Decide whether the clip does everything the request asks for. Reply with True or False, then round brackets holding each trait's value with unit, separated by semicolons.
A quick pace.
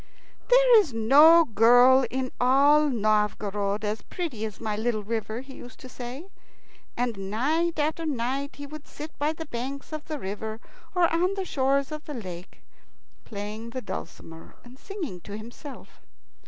False (160 wpm)